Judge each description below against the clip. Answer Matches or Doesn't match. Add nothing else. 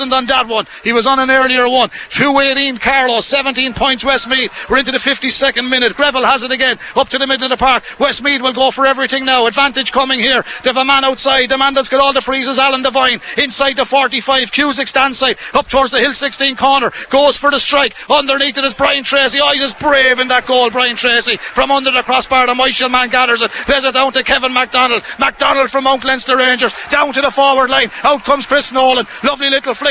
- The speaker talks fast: Matches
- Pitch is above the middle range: Matches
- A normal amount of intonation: Doesn't match